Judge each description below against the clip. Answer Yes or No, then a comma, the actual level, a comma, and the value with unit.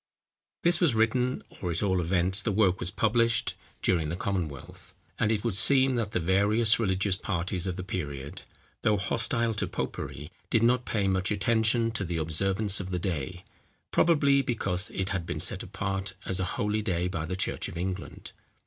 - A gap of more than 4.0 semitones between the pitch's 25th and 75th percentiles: No, average, 3.6 semitones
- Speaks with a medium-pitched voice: No, very low, 95 Hz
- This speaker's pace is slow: No, average, 185 wpm